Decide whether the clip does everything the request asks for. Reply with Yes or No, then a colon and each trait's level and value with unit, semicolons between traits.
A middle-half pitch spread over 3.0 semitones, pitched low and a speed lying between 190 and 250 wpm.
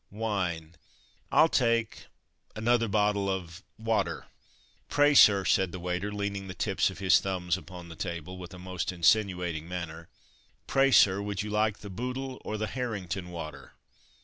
No: average, 3.4 semitones; very low, 95 Hz; average, 155 wpm